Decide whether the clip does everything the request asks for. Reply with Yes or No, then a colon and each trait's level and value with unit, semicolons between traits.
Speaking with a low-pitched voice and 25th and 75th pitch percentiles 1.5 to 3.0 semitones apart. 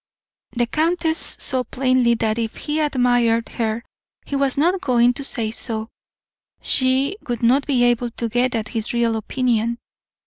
No: high, 245 Hz; average, 2.7 semitones